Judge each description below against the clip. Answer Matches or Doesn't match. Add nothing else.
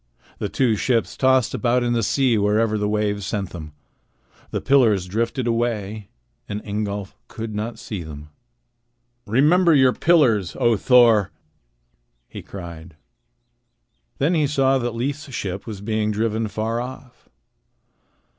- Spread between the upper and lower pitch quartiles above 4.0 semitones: Doesn't match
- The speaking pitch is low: Matches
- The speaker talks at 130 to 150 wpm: Matches